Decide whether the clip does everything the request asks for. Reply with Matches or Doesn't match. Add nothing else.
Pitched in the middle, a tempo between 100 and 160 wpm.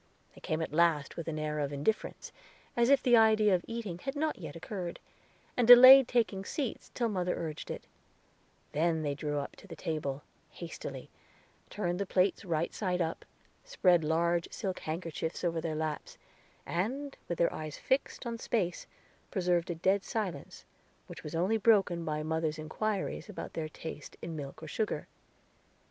Doesn't match